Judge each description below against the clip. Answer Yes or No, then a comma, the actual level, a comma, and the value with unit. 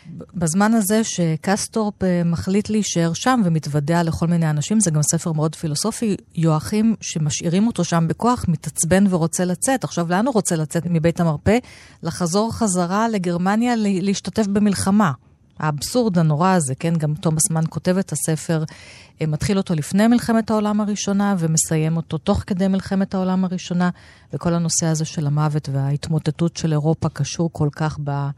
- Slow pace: No, average, 145 wpm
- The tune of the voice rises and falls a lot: No, average, 3.9 semitones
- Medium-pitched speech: Yes, medium, 170 Hz